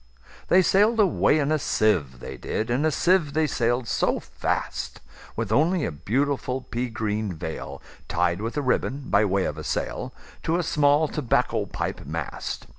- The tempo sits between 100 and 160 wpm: Yes, average, 155 wpm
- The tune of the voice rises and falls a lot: Yes, wide, 6.5 semitones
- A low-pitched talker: Yes, low, 125 Hz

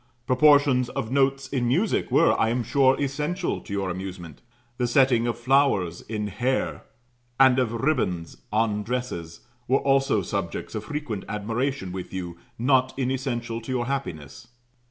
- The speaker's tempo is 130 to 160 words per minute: Yes, average, 150 wpm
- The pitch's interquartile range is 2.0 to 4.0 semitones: No, average, 4.5 semitones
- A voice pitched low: Yes, low, 125 Hz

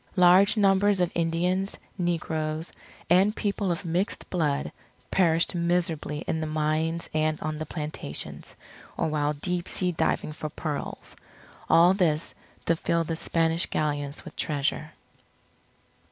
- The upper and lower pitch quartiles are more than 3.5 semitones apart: No, narrow, 2.6 semitones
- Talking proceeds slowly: Yes, slow, 130 wpm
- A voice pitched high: No, medium, 165 Hz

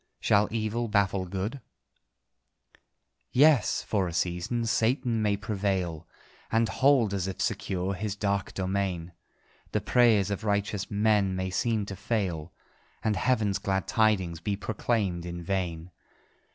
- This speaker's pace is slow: Yes, slow, 130 wpm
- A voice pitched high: No, low, 100 Hz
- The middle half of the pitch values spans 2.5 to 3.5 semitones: Yes, average, 2.8 semitones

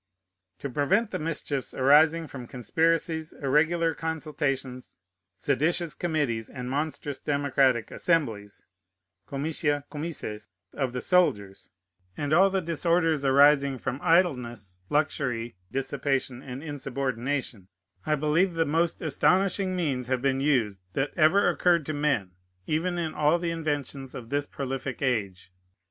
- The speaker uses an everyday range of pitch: Yes, average, 3.9 semitones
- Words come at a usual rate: No, slow, 125 wpm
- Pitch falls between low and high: Yes, medium, 145 Hz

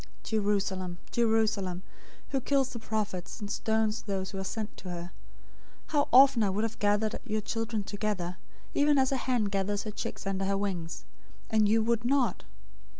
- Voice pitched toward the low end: No, high, 210 Hz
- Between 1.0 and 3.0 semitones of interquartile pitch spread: Yes, narrow, 2.6 semitones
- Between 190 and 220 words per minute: No, average, 175 wpm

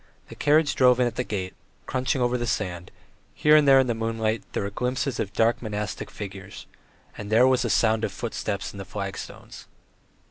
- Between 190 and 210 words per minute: Yes, fast, 205 wpm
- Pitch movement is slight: No, average, 3.7 semitones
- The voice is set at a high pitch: No, low, 115 Hz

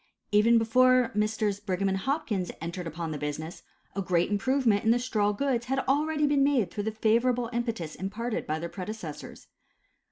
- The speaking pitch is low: No, high, 215 Hz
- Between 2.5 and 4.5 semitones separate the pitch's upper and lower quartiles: No, average, 4.9 semitones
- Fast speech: No, average, 170 wpm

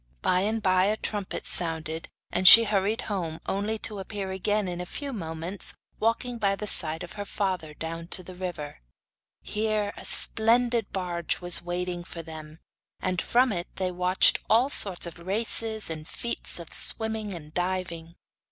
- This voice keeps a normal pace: Yes, average, 170 wpm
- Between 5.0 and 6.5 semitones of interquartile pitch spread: No, average, 3.7 semitones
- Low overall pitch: No, medium, 185 Hz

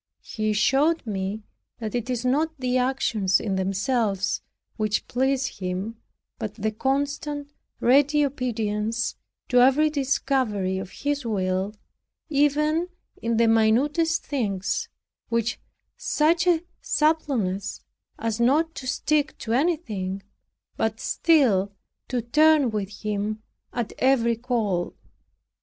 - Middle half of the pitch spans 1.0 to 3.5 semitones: No, average, 5.3 semitones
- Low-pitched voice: No, high, 240 Hz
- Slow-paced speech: Yes, slow, 115 wpm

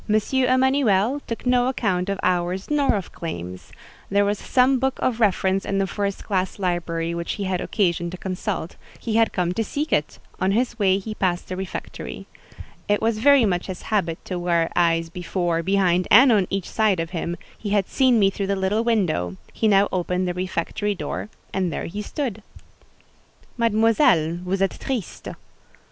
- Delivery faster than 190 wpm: No, average, 180 wpm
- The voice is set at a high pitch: Yes, high, 195 Hz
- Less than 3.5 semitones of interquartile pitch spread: No, average, 3.9 semitones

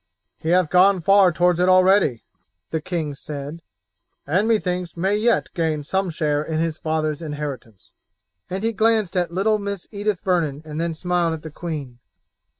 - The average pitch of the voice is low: No, medium, 175 Hz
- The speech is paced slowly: No, average, 165 wpm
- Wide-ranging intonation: No, average, 3.7 semitones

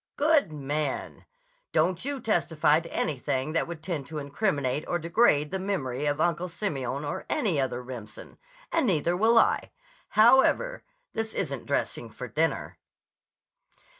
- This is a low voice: No, medium, 160 Hz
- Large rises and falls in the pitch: Yes, wide, 6.7 semitones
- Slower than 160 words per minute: Yes, average, 140 wpm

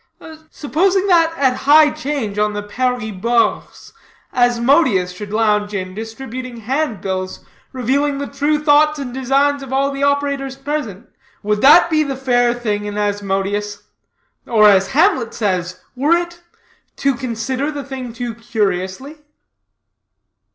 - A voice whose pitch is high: Yes, very high, 250 Hz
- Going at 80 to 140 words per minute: Yes, slow, 135 wpm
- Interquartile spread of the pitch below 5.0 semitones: No, average, 5.3 semitones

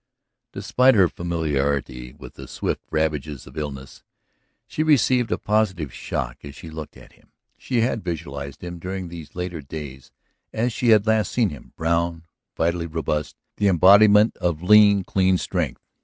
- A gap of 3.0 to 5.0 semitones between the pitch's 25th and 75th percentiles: No, wide, 5.5 semitones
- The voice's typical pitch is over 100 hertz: No, very low, 85 Hz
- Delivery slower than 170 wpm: Yes, average, 155 wpm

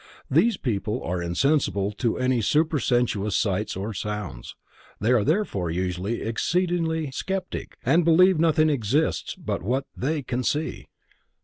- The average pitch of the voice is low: Yes, low, 125 Hz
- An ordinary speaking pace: No, slow, 130 wpm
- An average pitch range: No, wide, 7.4 semitones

